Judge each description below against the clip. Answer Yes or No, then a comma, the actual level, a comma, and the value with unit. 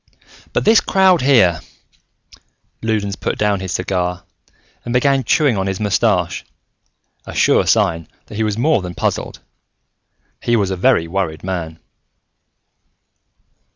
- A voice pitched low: Yes, low, 100 Hz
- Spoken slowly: Yes, slow, 130 wpm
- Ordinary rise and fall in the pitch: Yes, average, 4.8 semitones